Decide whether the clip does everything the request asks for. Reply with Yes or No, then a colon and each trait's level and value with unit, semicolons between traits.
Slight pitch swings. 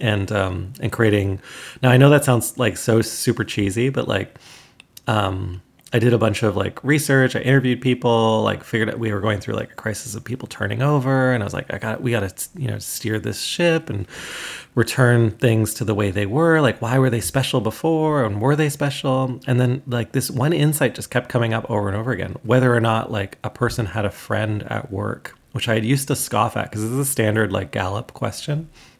No: average, 3.3 semitones